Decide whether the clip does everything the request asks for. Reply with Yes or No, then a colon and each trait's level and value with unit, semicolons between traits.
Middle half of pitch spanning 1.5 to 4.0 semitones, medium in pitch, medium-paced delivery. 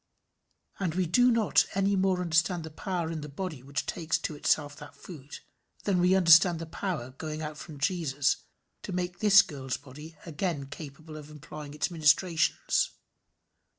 Yes: average, 3.5 semitones; medium, 160 Hz; average, 165 wpm